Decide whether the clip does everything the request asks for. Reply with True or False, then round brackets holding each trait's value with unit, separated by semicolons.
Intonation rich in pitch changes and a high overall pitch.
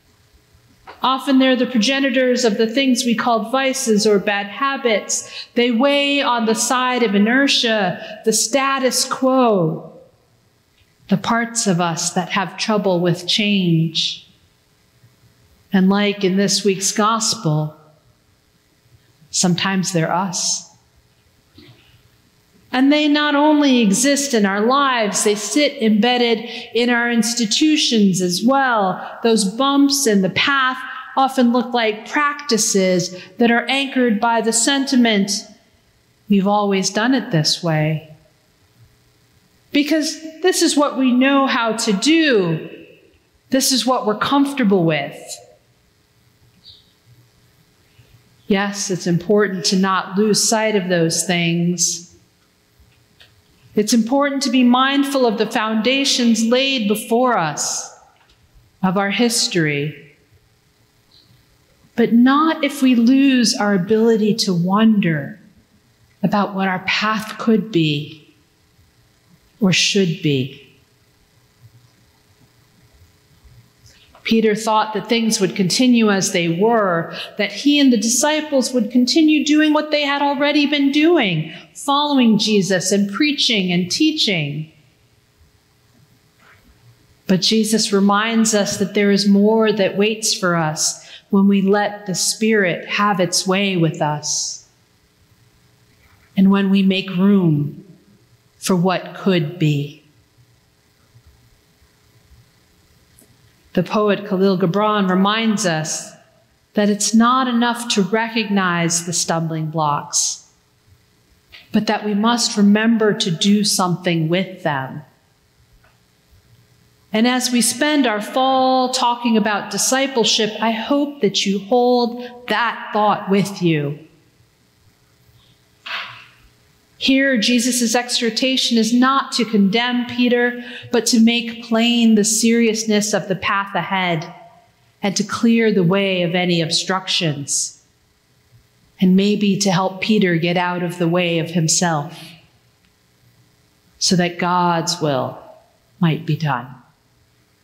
True (5.8 semitones; 205 Hz)